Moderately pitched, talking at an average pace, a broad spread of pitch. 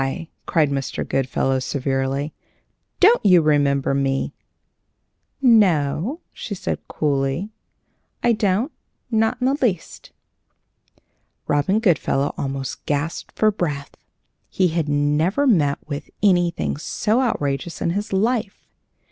No: medium, 160 Hz; slow, 110 wpm; wide, 6.8 semitones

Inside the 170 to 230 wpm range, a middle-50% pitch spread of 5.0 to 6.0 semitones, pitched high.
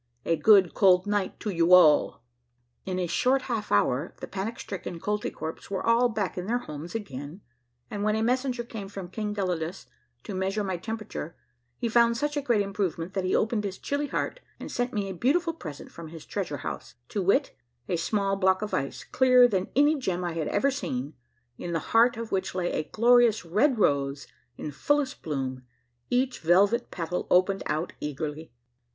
Yes: average, 190 wpm; wide, 5.4 semitones; high, 195 Hz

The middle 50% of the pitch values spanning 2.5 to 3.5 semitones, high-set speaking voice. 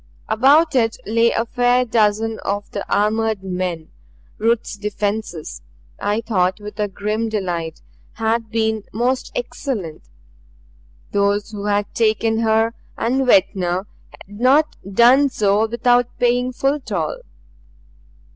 Yes: average, 2.8 semitones; high, 220 Hz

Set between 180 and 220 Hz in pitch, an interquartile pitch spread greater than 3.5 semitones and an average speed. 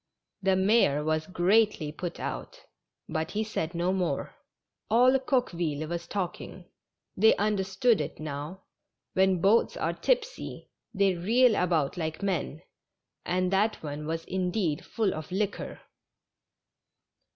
No: medium, 185 Hz; average, 4.6 semitones; slow, 125 wpm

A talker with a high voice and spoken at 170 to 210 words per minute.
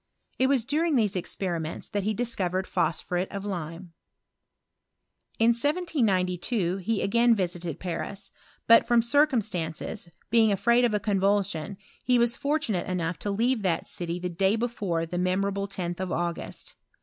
No: high, 195 Hz; average, 150 wpm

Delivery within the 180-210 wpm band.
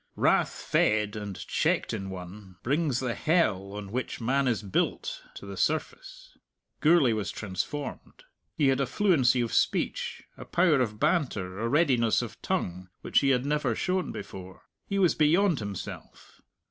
No: average, 160 wpm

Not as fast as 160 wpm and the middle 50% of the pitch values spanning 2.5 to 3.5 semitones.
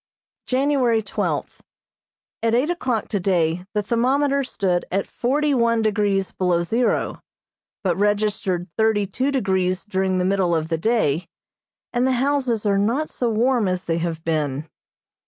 No: average, 145 wpm; average, 5.1 semitones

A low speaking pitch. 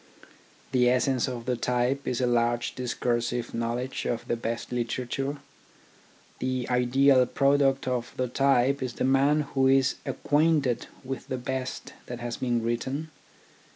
Yes: low, 125 Hz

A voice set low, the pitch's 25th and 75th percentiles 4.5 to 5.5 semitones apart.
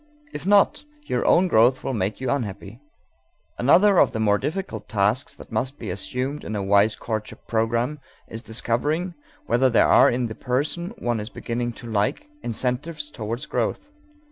Yes: low, 120 Hz; average, 4.9 semitones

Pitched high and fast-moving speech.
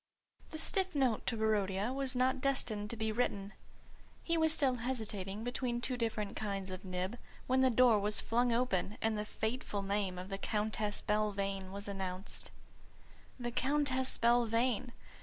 No: high, 220 Hz; average, 160 wpm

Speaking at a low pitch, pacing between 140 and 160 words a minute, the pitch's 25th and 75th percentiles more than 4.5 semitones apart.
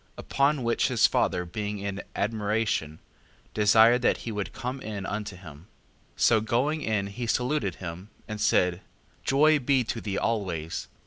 No: low, 110 Hz; average, 155 wpm; average, 3.8 semitones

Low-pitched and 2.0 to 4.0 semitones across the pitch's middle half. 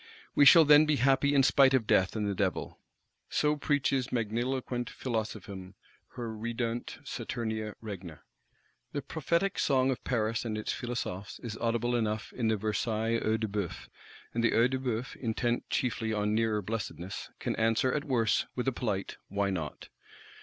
Yes: low, 115 Hz; average, 3.3 semitones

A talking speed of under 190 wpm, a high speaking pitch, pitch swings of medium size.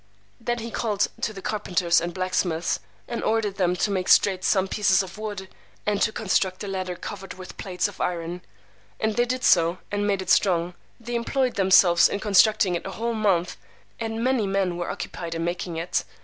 No: average, 195 wpm; high, 195 Hz; average, 3.2 semitones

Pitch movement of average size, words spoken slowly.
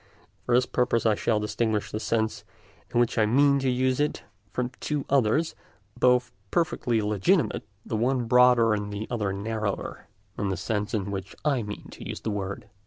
No: average, 3.1 semitones; average, 180 wpm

